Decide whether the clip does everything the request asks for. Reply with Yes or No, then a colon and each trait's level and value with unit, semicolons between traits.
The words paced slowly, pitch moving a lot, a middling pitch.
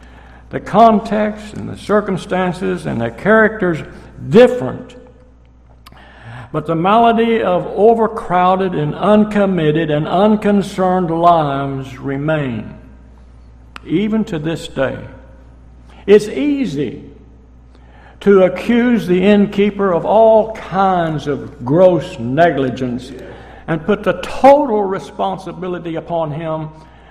Yes: slow, 95 wpm; wide, 7.9 semitones; medium, 170 Hz